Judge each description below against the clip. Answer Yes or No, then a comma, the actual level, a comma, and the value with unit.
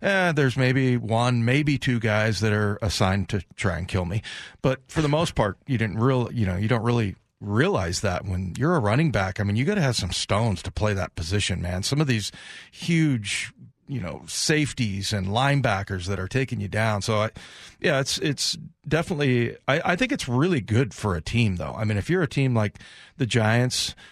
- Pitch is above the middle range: No, low, 115 Hz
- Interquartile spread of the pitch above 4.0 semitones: Yes, average, 5.0 semitones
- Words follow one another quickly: Yes, fast, 220 wpm